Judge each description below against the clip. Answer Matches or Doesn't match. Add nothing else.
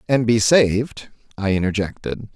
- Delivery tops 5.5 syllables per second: Doesn't match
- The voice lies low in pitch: Matches